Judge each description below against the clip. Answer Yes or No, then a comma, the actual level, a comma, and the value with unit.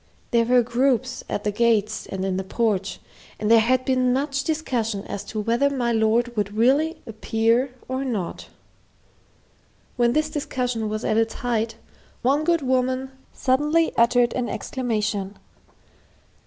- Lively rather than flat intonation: No, average, 3.0 semitones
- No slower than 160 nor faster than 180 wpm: No, average, 145 wpm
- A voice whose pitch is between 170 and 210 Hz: No, high, 240 Hz